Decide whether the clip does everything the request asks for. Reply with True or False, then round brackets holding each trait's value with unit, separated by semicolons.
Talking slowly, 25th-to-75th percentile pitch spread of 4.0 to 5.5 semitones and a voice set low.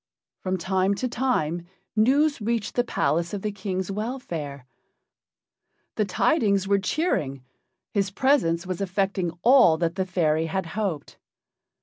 False (130 wpm; 4.5 semitones; 195 Hz)